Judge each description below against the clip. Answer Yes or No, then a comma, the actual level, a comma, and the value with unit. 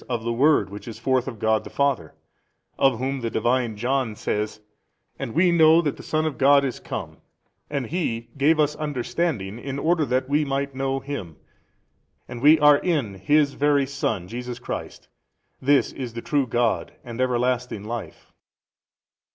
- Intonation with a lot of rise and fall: No, average, 3.6 semitones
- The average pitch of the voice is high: No, low, 130 Hz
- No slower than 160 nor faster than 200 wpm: Yes, average, 175 wpm